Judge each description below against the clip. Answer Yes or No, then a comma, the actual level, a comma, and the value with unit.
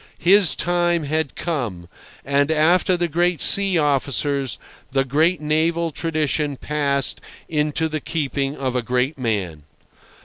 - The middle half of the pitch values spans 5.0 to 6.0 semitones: No, average, 3.3 semitones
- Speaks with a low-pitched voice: No, medium, 150 Hz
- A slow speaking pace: Yes, slow, 130 wpm